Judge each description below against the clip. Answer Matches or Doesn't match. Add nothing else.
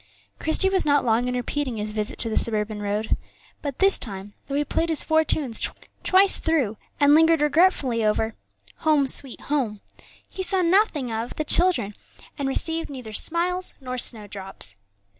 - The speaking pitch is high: Matches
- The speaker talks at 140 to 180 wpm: Matches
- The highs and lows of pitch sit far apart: Matches